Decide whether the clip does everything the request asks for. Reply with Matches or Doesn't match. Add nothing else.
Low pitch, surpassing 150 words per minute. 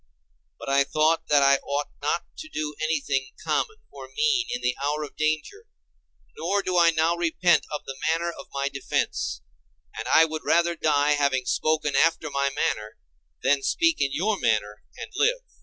Doesn't match